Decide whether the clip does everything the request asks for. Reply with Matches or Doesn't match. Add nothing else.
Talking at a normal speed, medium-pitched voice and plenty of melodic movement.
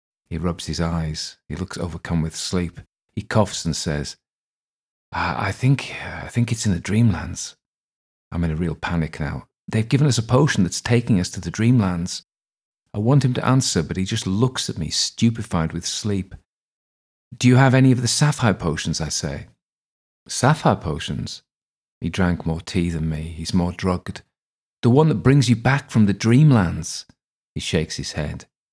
Doesn't match